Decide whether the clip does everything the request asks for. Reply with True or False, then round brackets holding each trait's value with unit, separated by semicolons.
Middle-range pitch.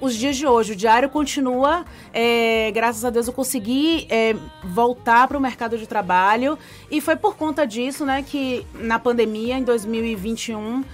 False (245 Hz)